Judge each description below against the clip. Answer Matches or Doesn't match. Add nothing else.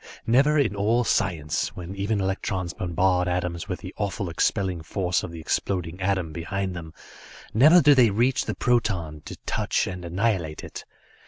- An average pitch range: Matches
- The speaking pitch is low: Matches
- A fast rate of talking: Doesn't match